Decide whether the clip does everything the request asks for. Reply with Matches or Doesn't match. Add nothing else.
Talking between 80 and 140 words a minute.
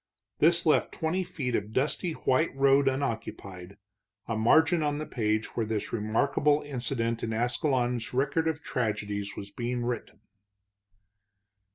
Matches